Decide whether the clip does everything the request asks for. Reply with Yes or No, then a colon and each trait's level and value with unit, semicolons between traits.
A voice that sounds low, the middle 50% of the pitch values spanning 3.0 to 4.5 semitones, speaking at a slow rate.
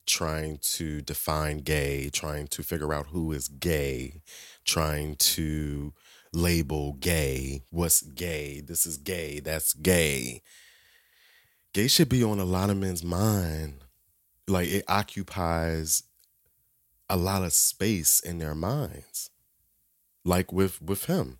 Yes: very low, 80 Hz; average, 3.5 semitones; slow, 125 wpm